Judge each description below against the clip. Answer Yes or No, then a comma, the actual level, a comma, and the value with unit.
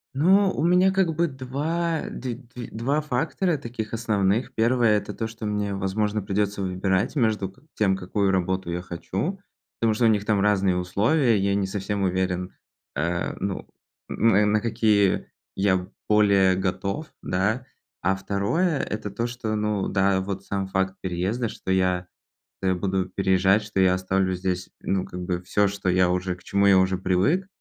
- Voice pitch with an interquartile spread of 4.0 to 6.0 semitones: No, average, 3.5 semitones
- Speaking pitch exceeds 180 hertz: No, low, 100 Hz